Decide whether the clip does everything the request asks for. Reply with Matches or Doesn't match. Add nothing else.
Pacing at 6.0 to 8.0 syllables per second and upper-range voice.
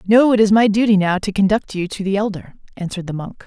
Matches